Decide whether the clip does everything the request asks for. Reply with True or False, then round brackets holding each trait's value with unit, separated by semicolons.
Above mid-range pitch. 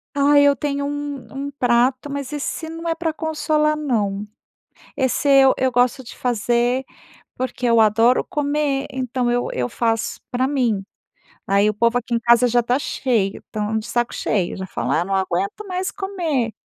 True (250 Hz)